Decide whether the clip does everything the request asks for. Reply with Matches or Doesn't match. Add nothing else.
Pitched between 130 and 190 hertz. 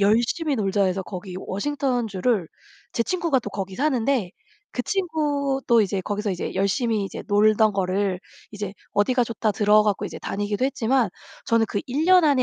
Doesn't match